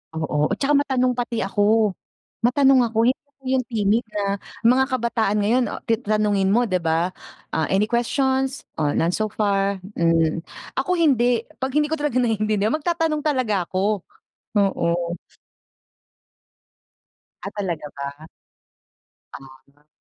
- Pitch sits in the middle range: No, high, 215 Hz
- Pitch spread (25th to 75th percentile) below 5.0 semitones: No, wide, 5.6 semitones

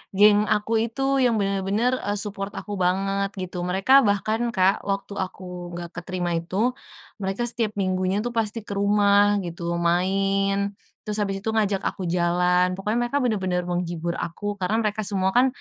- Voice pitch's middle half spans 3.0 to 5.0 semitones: No, narrow, 2.5 semitones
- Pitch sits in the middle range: No, high, 195 Hz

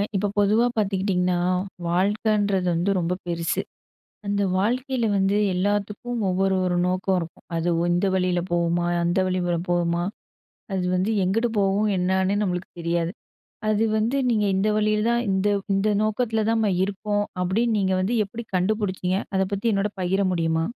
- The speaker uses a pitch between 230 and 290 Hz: No, high, 195 Hz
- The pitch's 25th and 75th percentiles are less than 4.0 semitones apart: Yes, average, 2.7 semitones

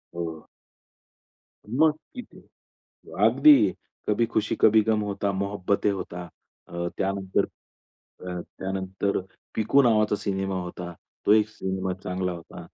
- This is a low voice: Yes, low, 100 Hz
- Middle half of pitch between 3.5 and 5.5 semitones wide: No, average, 2.7 semitones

